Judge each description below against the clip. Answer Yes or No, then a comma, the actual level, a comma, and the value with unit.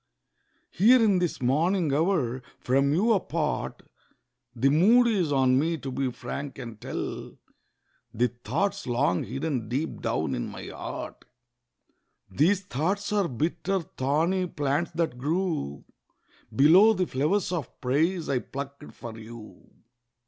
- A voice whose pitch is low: No, medium, 150 Hz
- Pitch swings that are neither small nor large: No, wide, 5.9 semitones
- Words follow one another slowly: Yes, slow, 125 wpm